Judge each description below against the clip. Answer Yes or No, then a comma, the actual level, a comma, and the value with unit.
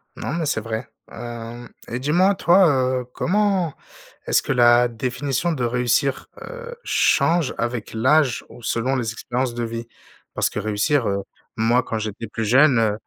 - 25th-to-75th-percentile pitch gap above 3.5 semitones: Yes, average, 4.2 semitones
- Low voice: Yes, low, 125 Hz